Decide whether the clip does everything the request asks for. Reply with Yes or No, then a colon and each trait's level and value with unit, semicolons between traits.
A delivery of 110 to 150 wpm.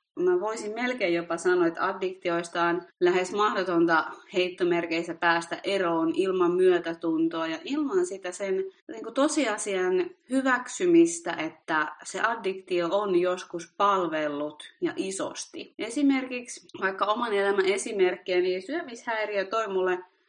Yes: average, 120 wpm